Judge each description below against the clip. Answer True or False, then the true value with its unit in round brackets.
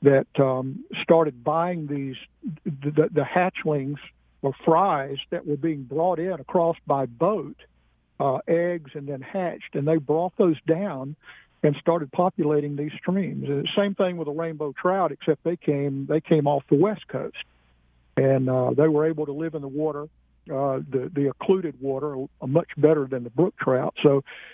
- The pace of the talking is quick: False (175 wpm)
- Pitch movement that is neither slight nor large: True (3.3 semitones)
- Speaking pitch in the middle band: True (150 Hz)